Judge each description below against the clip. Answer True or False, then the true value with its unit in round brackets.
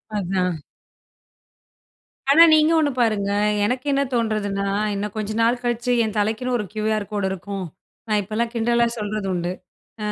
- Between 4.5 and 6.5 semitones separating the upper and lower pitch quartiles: False (2.8 semitones)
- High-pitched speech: True (215 Hz)